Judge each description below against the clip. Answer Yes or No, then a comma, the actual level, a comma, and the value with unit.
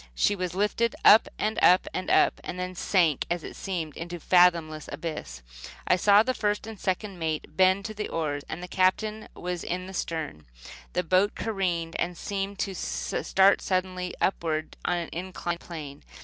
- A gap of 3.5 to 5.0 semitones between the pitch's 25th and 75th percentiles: No, average, 2.8 semitones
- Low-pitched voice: No, medium, 180 Hz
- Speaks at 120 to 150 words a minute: No, average, 175 wpm